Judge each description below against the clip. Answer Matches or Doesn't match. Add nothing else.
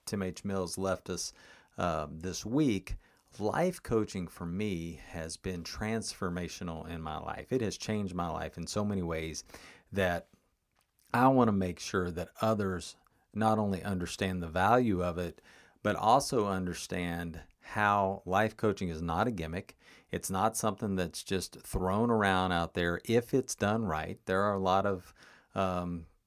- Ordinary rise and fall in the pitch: Matches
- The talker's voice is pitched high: Doesn't match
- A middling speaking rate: Matches